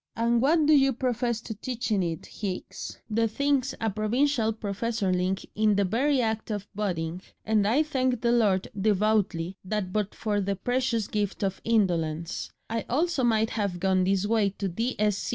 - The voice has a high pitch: Yes, high, 215 Hz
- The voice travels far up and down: No, average, 3.5 semitones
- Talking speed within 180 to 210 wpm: No, average, 170 wpm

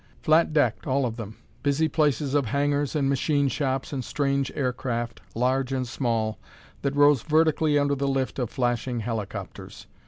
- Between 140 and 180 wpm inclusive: Yes, average, 160 wpm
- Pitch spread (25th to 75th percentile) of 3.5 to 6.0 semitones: No, average, 2.9 semitones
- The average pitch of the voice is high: No, low, 135 Hz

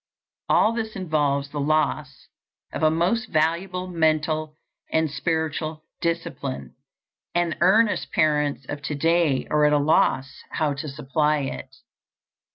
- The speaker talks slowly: Yes, slow, 130 wpm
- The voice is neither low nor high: Yes, medium, 155 Hz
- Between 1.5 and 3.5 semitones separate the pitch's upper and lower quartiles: Yes, narrow, 2.4 semitones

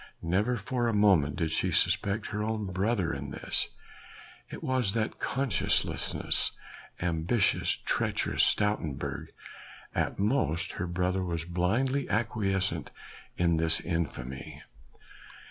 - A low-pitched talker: Yes, very low, 95 Hz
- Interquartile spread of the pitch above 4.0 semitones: Yes, average, 4.6 semitones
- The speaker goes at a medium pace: No, slow, 110 wpm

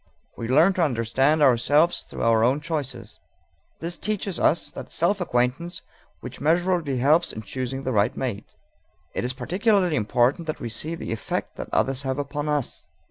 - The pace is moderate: Yes, average, 170 wpm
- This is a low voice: No, medium, 145 Hz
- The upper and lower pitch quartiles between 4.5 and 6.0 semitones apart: Yes, average, 5.2 semitones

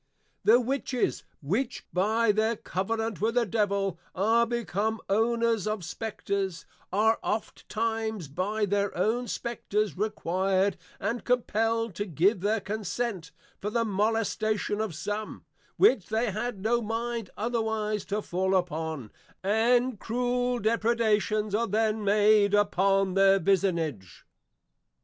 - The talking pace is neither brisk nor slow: No, slow, 120 wpm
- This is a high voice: Yes, high, 215 Hz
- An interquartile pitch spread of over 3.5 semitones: No, average, 2.7 semitones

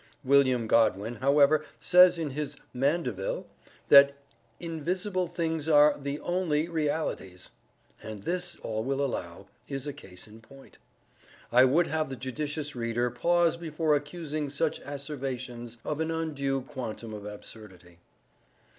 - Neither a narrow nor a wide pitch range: Yes, average, 4.7 semitones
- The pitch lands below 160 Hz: Yes, medium, 140 Hz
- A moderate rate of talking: No, slow, 130 wpm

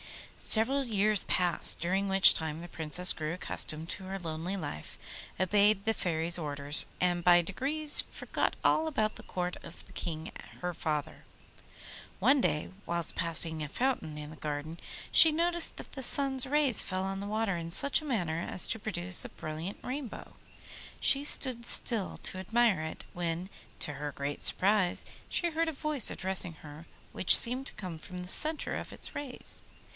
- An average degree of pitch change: No, wide, 6.5 semitones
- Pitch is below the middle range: No, medium, 185 Hz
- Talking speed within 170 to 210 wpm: Yes, average, 175 wpm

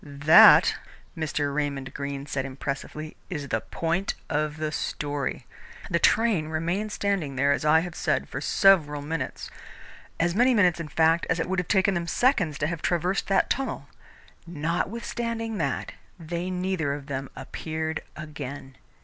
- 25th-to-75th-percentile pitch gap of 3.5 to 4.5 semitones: Yes, average, 3.9 semitones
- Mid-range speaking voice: Yes, medium, 160 Hz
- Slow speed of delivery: No, average, 155 wpm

